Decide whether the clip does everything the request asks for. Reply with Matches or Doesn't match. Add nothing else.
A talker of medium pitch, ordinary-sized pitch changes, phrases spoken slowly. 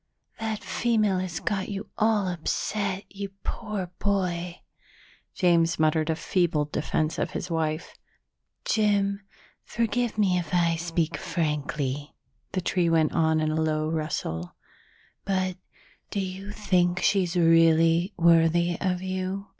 Matches